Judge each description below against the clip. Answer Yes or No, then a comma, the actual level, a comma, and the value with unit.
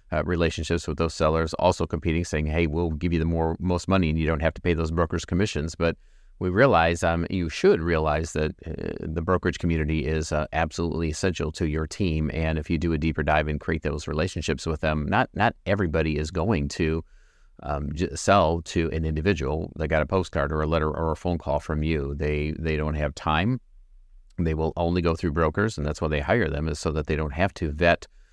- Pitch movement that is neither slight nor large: No, narrow, 1.8 semitones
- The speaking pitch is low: Yes, very low, 80 Hz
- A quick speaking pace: Yes, fast, 225 wpm